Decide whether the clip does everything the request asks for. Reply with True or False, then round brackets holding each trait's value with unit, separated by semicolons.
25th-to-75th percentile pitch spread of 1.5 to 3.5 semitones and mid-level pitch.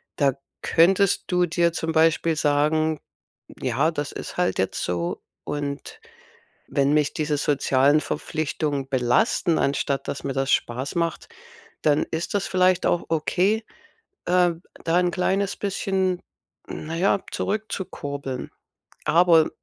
False (3.9 semitones; 160 Hz)